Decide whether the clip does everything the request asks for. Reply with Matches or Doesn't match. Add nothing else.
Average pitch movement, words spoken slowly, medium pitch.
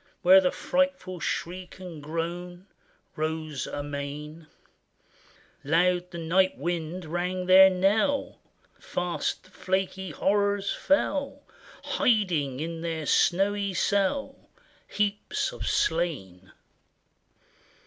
Matches